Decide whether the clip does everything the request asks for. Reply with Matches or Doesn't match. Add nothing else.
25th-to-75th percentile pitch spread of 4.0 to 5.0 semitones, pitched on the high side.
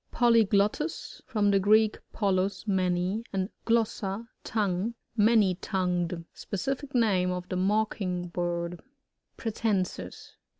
Doesn't match